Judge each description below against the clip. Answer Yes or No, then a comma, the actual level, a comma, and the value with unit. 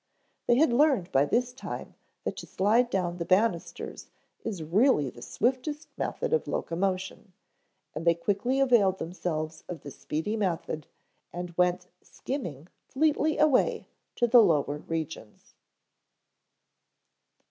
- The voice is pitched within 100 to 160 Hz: No, high, 190 Hz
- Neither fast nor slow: No, slow, 125 wpm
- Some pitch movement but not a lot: No, wide, 7.0 semitones